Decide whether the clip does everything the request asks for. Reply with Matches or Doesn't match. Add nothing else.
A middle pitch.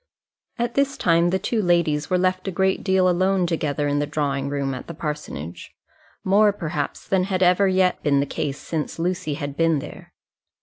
Matches